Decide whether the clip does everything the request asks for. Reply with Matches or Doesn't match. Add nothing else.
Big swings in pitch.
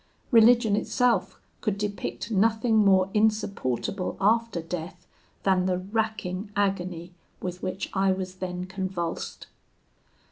Doesn't match